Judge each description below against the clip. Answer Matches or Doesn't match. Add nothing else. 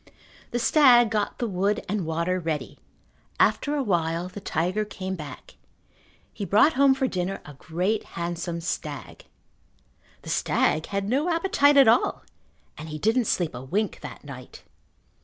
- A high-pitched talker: Matches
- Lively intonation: Matches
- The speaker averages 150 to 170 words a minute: Matches